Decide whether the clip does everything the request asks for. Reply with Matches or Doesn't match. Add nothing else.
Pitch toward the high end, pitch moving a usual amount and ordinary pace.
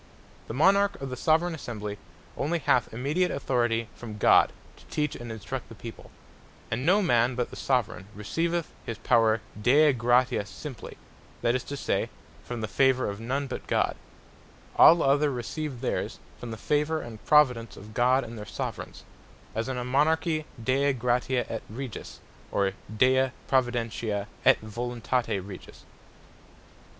Doesn't match